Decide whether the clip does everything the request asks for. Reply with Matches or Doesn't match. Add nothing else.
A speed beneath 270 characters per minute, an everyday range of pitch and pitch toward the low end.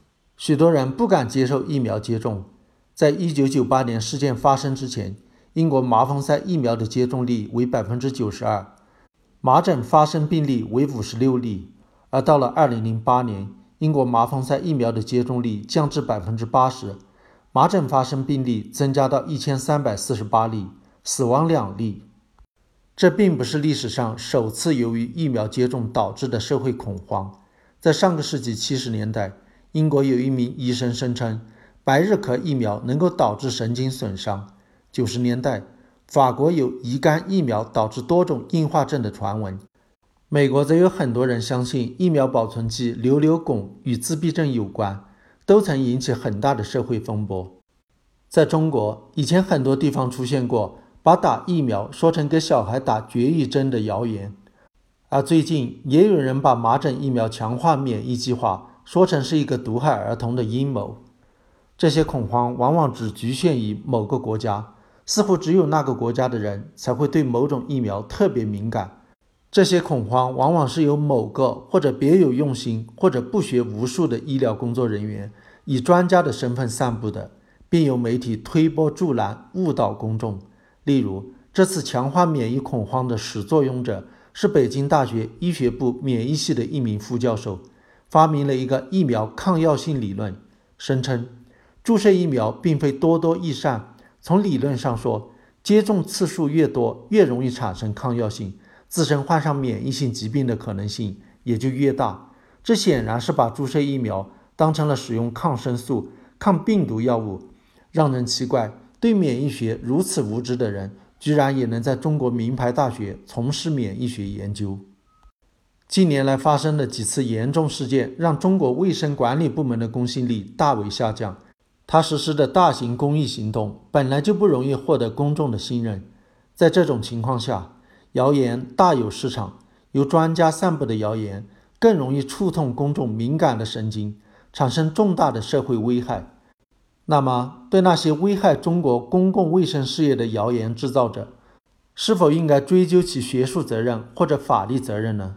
Matches